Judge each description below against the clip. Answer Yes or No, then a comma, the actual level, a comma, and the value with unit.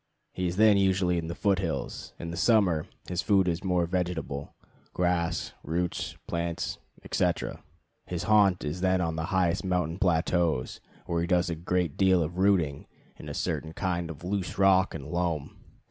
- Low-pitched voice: Yes, very low, 90 Hz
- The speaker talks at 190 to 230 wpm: No, average, 175 wpm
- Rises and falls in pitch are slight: Yes, narrow, 2.1 semitones